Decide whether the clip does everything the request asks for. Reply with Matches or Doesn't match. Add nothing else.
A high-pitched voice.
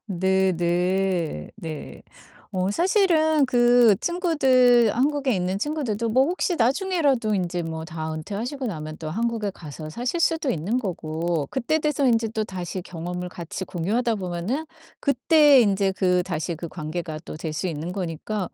Matches